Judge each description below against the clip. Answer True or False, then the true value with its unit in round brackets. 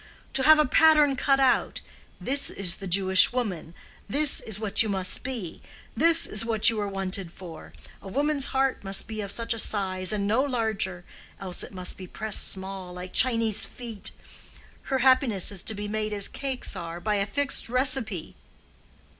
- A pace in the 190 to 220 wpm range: False (180 wpm)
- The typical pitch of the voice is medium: False (215 Hz)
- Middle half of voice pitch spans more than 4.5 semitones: True (5.1 semitones)